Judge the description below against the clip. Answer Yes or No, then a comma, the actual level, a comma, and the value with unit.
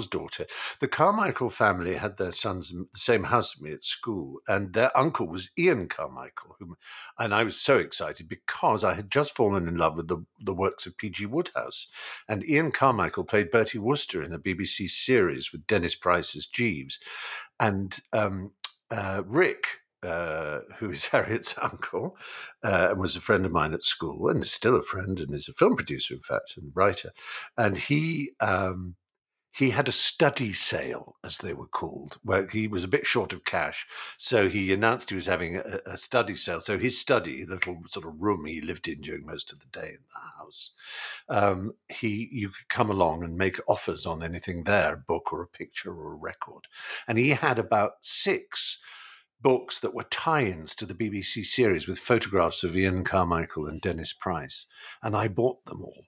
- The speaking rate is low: No, average, 195 wpm